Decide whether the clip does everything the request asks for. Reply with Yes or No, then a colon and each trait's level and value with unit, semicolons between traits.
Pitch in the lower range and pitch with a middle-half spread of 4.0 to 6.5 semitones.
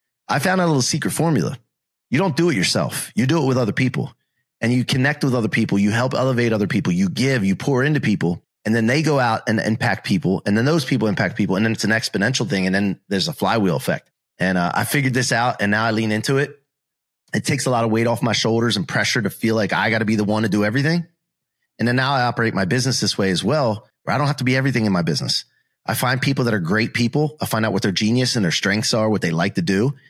Yes: low, 120 Hz; average, 4.3 semitones